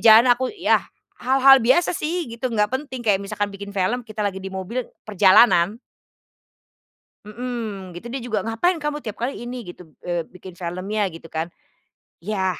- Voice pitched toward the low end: No, high, 215 Hz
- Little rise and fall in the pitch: No, average, 4.7 semitones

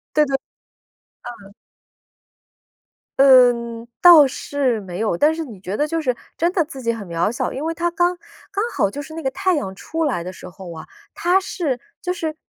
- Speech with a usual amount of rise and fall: No, wide, 6.9 semitones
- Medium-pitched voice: No, very high, 275 Hz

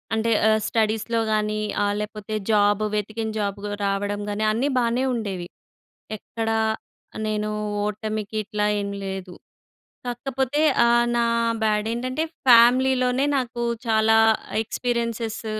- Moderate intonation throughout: No, narrow, 2.1 semitones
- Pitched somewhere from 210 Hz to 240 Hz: Yes, high, 220 Hz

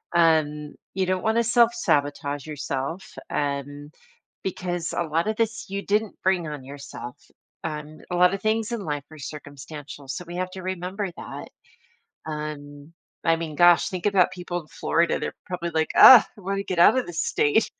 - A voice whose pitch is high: No, medium, 170 Hz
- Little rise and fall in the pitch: No, average, 4.2 semitones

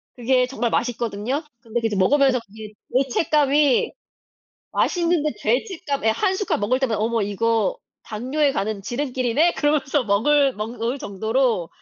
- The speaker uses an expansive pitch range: No, average, 4.6 semitones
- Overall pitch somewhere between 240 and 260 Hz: Yes, high, 245 Hz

